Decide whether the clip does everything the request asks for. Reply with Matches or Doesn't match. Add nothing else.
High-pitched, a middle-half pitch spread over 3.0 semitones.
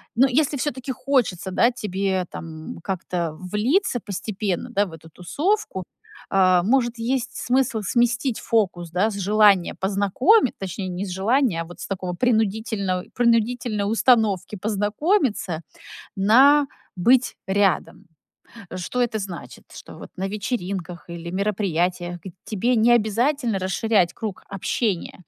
Matches